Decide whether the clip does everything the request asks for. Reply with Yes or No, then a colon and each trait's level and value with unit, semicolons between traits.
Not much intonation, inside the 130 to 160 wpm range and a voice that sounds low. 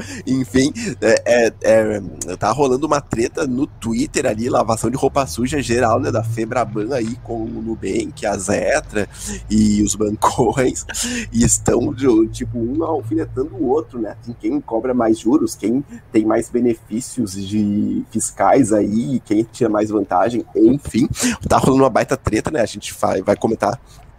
No: average, 3.6 semitones; average, 155 wpm; low, 115 Hz